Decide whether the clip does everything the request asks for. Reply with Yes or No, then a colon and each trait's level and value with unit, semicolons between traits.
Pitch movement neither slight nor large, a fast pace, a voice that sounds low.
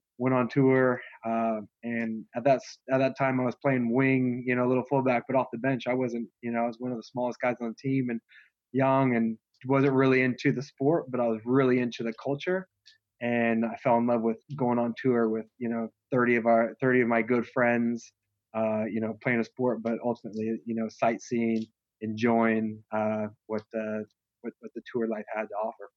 No: narrow, 2.2 semitones; fast, 220 wpm; low, 120 Hz